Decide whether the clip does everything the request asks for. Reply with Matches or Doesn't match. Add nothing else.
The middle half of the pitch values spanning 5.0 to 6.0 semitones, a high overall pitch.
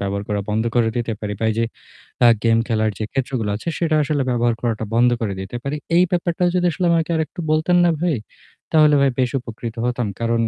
Doesn't match